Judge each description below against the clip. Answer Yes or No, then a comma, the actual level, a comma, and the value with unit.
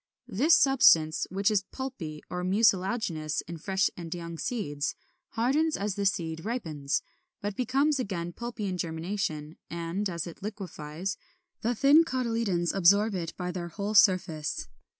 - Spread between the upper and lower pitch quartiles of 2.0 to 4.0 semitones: No, average, 5.0 semitones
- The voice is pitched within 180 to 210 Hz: Yes, high, 190 Hz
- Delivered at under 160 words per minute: Yes, average, 145 wpm